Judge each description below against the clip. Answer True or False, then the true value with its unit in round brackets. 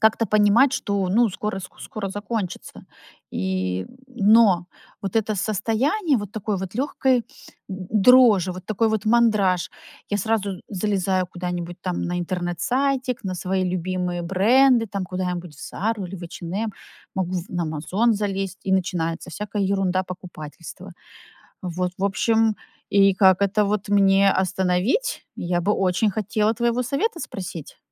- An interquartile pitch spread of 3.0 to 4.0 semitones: True (3.3 semitones)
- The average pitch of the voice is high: True (195 Hz)